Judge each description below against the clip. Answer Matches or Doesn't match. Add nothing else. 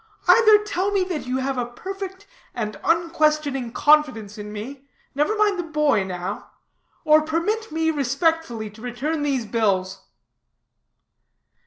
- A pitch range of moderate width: Doesn't match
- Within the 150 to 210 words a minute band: Doesn't match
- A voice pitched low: Doesn't match